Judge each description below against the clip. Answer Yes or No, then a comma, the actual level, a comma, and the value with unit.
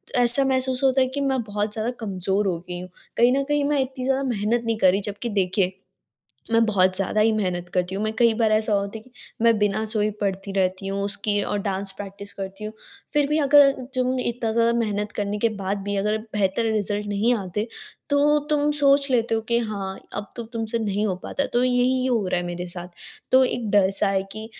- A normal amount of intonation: Yes, average, 3.8 semitones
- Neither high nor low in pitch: No, high, 215 Hz